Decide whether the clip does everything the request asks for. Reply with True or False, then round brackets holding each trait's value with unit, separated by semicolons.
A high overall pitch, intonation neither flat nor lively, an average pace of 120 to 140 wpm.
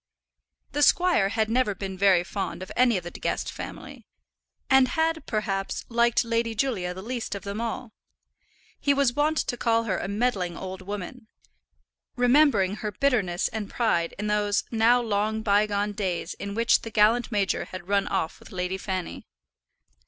False (210 Hz; 3.7 semitones; 170 wpm)